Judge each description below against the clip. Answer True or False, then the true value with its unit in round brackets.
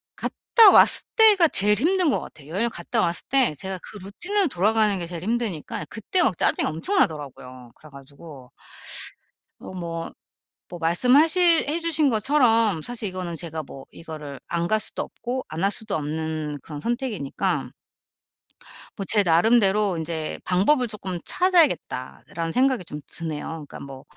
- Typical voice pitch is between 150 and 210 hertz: True (190 Hz)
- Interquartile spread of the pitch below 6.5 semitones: False (7.6 semitones)